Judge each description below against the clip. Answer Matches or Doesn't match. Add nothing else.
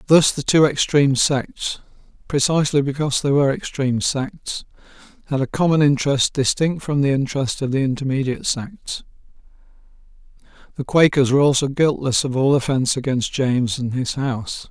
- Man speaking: Matches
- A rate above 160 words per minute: Doesn't match